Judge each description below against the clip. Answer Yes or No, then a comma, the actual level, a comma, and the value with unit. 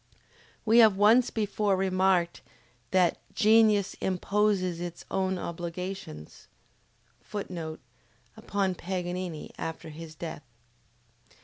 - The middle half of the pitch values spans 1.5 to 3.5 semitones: Yes, average, 2.9 semitones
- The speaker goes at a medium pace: No, slow, 90 wpm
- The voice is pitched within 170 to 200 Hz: Yes, medium, 185 Hz